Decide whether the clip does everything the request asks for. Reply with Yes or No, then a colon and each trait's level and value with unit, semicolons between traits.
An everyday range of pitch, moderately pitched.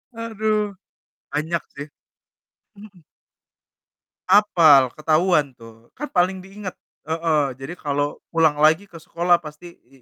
Yes: average, 4.0 semitones; medium, 165 Hz